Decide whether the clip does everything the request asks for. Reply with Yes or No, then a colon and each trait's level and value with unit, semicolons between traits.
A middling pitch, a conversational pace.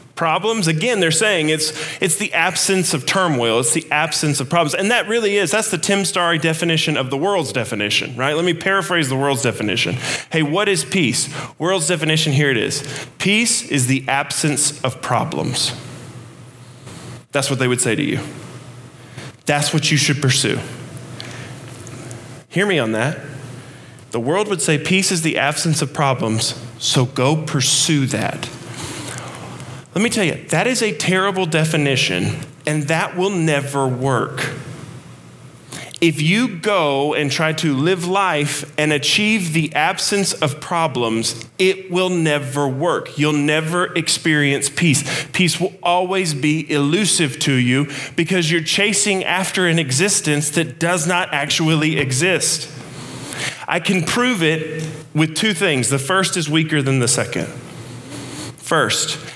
Yes: medium, 150 Hz; average, 150 wpm